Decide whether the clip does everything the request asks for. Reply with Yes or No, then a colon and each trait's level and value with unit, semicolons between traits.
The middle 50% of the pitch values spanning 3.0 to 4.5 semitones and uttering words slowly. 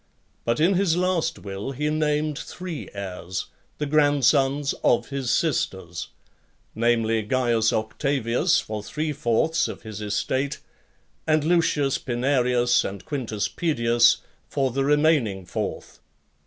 No: average, 5.1 semitones; slow, 120 wpm